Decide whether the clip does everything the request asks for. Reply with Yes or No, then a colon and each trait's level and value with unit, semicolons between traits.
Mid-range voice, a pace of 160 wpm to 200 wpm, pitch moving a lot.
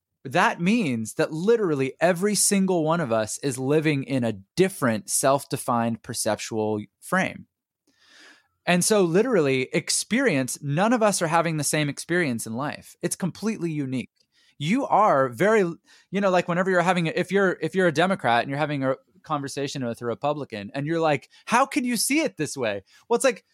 Yes: medium, 160 Hz; average, 180 wpm; wide, 5.9 semitones